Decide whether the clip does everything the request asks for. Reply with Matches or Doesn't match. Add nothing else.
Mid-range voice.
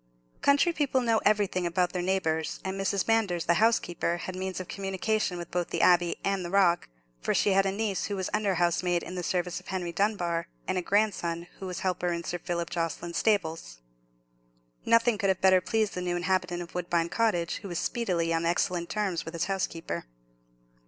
Matches